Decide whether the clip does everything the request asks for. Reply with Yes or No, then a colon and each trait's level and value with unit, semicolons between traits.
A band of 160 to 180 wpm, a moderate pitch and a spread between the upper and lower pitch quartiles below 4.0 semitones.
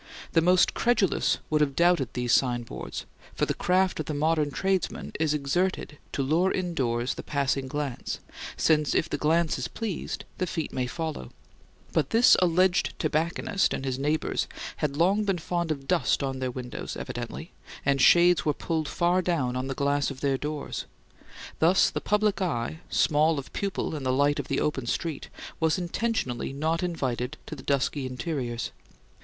No: average, 170 wpm; medium, 155 Hz; average, 4.3 semitones